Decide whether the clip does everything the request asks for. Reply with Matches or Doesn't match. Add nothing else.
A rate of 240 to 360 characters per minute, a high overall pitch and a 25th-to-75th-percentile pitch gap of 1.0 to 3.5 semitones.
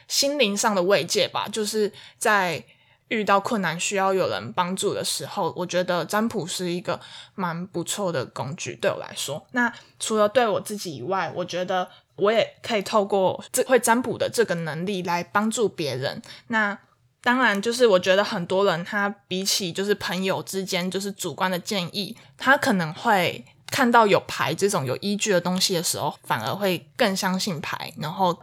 Matches